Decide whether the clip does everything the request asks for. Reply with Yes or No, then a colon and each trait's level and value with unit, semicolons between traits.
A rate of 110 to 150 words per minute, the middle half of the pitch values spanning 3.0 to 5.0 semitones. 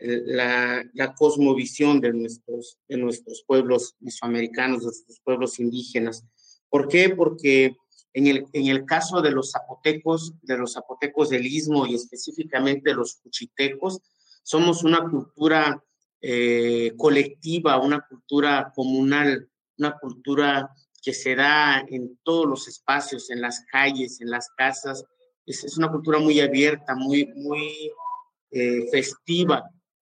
Yes: average, 130 wpm; average, 3.3 semitones